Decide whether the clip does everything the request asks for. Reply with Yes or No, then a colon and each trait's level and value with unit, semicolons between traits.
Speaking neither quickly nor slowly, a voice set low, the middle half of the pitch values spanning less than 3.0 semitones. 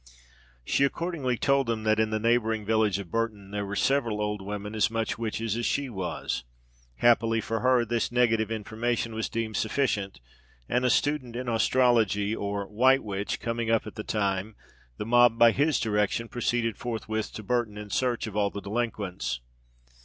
Yes: average, 175 wpm; low, 110 Hz; narrow, 2.5 semitones